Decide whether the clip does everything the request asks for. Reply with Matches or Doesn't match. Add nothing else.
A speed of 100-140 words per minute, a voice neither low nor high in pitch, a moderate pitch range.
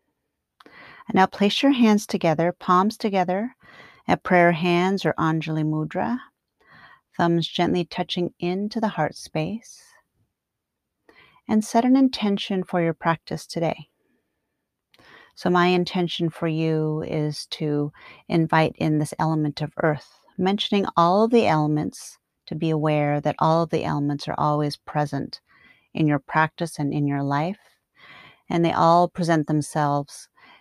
Matches